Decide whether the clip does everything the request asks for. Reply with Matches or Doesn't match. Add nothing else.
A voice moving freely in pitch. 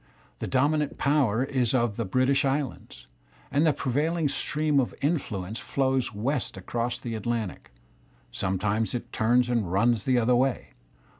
Doesn't match